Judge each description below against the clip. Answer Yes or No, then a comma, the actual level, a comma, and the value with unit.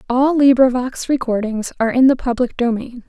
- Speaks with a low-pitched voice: No, very high, 250 Hz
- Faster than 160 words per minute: No, average, 155 wpm